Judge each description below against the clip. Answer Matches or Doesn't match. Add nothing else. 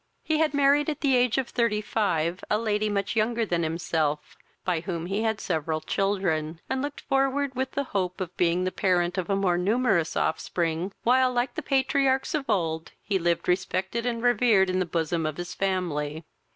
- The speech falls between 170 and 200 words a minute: Matches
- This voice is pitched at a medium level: Doesn't match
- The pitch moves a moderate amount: Doesn't match